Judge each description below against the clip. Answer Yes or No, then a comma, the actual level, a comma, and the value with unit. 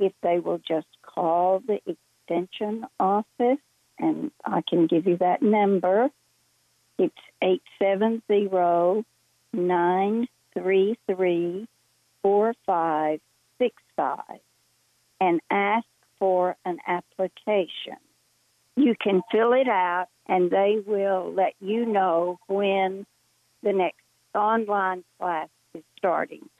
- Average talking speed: No, slow, 90 wpm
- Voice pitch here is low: No, high, 190 Hz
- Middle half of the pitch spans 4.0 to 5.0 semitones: No, average, 3.0 semitones